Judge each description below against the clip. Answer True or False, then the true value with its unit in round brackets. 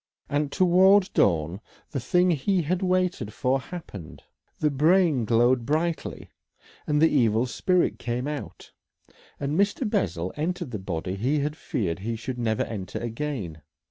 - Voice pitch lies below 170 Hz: True (135 Hz)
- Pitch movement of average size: False (7.5 semitones)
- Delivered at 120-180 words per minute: True (145 wpm)